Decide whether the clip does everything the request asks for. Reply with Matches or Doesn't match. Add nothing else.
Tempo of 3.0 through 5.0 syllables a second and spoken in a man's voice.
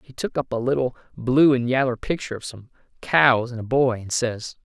Doesn't match